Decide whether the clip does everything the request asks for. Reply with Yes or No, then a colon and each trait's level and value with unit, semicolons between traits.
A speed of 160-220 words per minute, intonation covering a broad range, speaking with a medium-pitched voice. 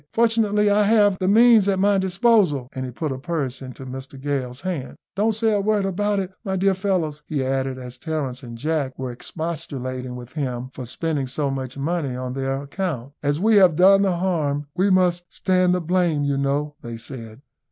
Yes: average, 200 wpm; wide, 6.3 semitones; medium, 155 Hz